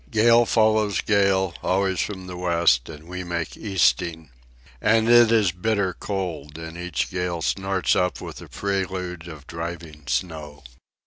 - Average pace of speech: Yes, average, 145 wpm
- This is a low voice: Yes, very low, 90 Hz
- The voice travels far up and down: No, average, 3.1 semitones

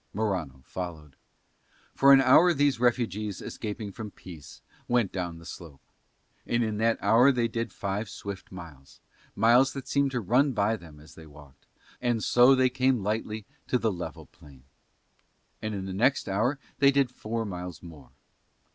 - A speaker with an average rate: Yes, average, 165 wpm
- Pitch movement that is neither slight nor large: No, wide, 5.7 semitones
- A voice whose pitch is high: No, low, 110 Hz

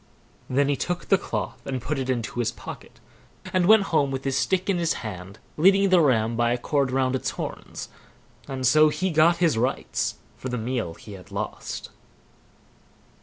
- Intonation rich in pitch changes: Yes, wide, 5.7 semitones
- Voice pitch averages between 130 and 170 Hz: Yes, low, 135 Hz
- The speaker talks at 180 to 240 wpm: Yes, average, 185 wpm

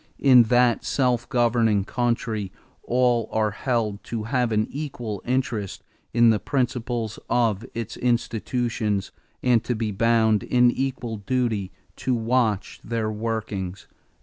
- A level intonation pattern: Yes, narrow, 2.2 semitones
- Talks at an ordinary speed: No, slow, 125 wpm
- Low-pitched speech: Yes, low, 115 Hz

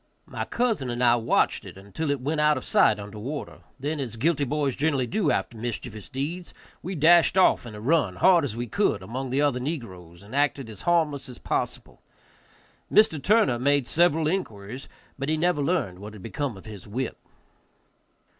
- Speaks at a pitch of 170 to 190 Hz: No, low, 135 Hz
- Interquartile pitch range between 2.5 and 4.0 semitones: No, wide, 5.5 semitones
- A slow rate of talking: No, average, 185 wpm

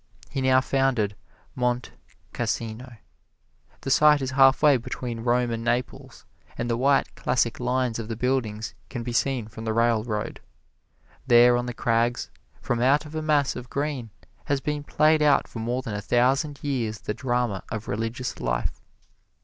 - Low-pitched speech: Yes, low, 125 Hz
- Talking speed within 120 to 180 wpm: Yes, average, 165 wpm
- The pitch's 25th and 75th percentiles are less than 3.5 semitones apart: Yes, average, 2.7 semitones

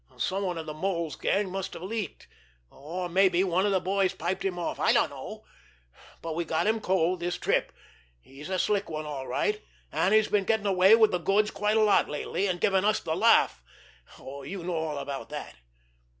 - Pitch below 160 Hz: No, medium, 185 Hz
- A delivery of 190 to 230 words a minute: Yes, average, 200 wpm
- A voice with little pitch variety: No, average, 3.3 semitones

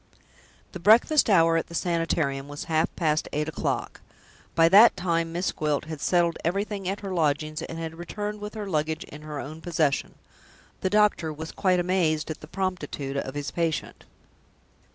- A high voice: No, medium, 165 Hz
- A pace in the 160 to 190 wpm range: Yes, average, 175 wpm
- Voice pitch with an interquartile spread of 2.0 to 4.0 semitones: Yes, average, 3.4 semitones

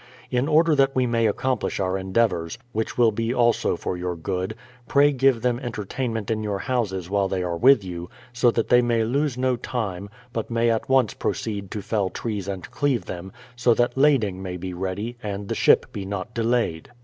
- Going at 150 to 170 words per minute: No, average, 200 wpm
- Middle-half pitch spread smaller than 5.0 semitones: Yes, average, 4.3 semitones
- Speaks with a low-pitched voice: Yes, low, 110 Hz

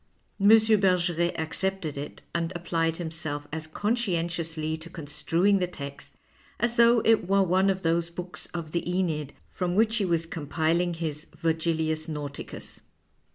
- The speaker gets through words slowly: No, average, 155 wpm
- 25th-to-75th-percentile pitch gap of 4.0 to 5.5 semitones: No, average, 2.9 semitones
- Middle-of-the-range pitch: Yes, medium, 170 Hz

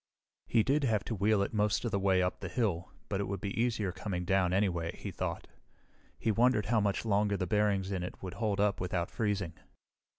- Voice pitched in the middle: No, low, 100 Hz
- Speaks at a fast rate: Yes, fast, 220 wpm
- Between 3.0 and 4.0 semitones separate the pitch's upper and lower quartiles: No, narrow, 2.5 semitones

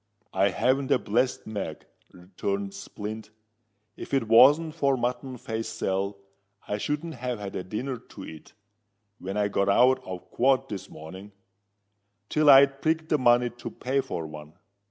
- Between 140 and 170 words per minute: Yes, average, 155 wpm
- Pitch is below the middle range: Yes, low, 115 Hz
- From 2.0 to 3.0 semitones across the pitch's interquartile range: No, average, 5.3 semitones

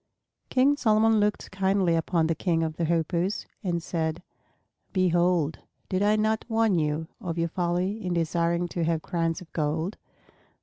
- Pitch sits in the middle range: Yes, medium, 175 Hz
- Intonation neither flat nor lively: Yes, average, 3.1 semitones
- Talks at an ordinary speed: Yes, average, 160 wpm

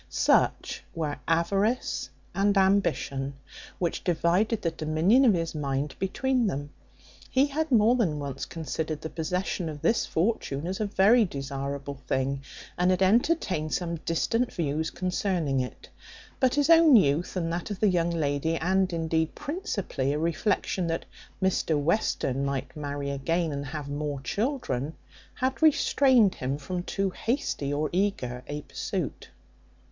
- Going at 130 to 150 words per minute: Yes, average, 145 wpm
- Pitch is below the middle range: No, medium, 170 Hz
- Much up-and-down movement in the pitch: Yes, wide, 5.9 semitones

